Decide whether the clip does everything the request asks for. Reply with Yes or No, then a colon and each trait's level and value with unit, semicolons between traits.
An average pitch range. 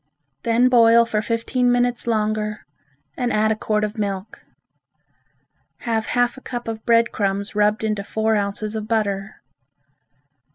No: narrow, 1.7 semitones